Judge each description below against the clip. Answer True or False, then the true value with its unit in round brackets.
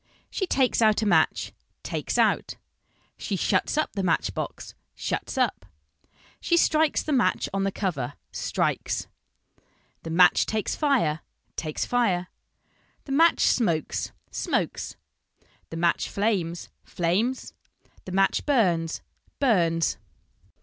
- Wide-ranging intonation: True (6.9 semitones)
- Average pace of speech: False (120 wpm)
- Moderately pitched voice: False (195 Hz)